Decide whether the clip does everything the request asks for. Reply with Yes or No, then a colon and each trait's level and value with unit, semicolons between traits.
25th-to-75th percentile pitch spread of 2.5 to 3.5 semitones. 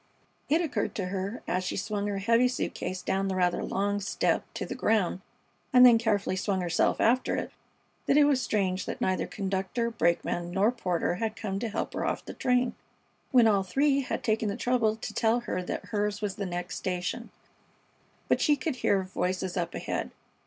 No: average, 3.9 semitones